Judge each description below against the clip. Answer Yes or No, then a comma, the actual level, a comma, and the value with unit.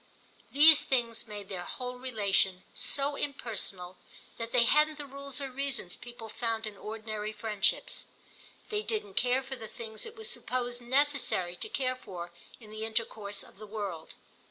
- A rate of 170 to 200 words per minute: No, average, 160 wpm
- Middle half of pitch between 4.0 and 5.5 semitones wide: Yes, average, 4.5 semitones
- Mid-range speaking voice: No, high, 235 Hz